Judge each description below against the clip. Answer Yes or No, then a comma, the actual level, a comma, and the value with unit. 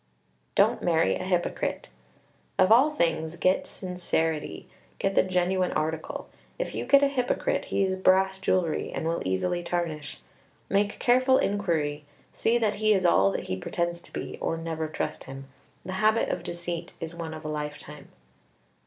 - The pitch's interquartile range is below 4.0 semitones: Yes, average, 3.4 semitones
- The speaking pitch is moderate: Yes, medium, 175 Hz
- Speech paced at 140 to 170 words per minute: Yes, average, 165 wpm